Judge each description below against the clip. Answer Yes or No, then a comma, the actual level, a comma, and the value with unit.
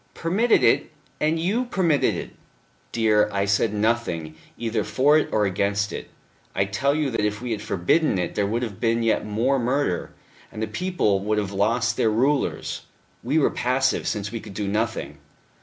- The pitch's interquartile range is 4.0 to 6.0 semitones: Yes, average, 5.2 semitones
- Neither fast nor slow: Yes, average, 180 wpm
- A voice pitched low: Yes, low, 115 Hz